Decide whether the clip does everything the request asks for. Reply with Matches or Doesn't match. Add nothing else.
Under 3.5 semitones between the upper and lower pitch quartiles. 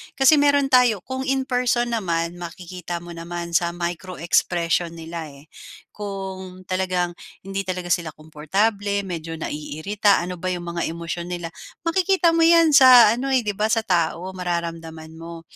Doesn't match